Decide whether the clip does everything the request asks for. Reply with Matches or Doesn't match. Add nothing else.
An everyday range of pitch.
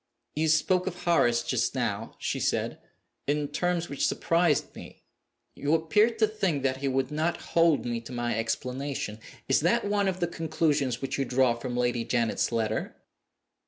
Doesn't match